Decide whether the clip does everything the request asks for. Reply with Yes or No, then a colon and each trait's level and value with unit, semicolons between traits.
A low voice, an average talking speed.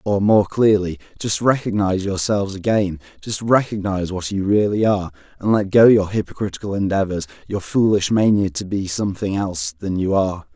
Yes: low, 100 Hz; average, 165 wpm